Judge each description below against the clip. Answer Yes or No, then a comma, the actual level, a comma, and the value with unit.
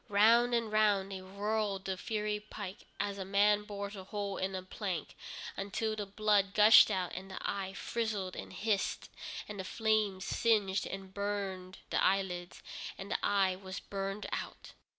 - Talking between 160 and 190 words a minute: Yes, average, 170 wpm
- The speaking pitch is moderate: No, high, 200 Hz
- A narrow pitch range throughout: Yes, narrow, 1.8 semitones